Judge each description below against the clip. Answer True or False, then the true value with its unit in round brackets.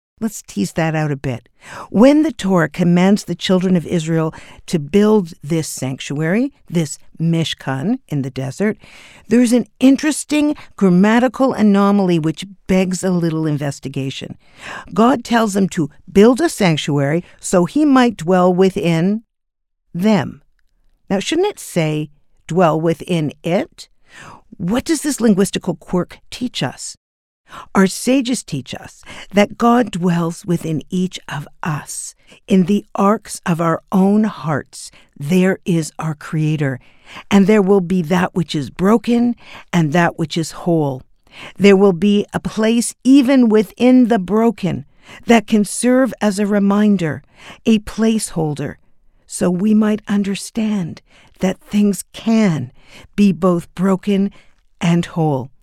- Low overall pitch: False (190 Hz)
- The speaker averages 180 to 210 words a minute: False (135 wpm)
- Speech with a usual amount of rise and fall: True (4.6 semitones)